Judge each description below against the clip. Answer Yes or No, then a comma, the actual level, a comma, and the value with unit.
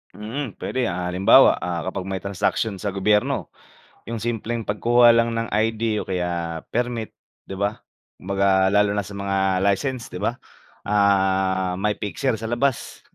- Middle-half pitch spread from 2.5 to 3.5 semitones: Yes, average, 3.2 semitones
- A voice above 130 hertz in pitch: No, low, 100 Hz